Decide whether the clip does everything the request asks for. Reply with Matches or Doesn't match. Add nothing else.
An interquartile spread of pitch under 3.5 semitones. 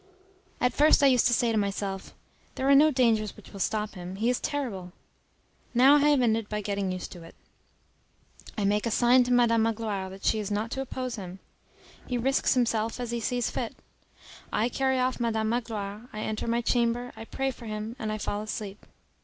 Matches